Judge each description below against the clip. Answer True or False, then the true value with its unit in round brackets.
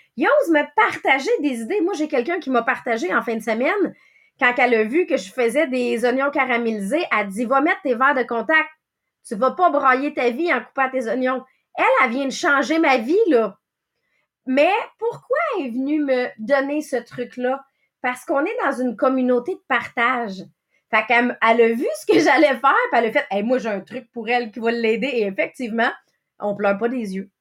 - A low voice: False (260 Hz)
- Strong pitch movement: False (3.7 semitones)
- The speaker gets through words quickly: True (220 wpm)